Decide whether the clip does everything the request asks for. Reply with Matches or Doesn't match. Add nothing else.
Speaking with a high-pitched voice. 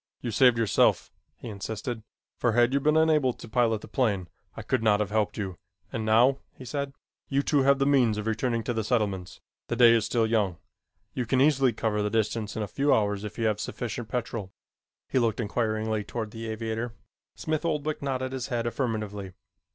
Doesn't match